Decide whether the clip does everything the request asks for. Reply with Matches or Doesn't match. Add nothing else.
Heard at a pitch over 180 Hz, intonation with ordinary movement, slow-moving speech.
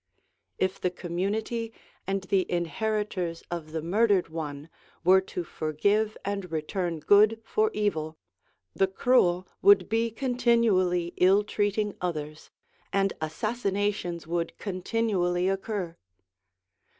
Matches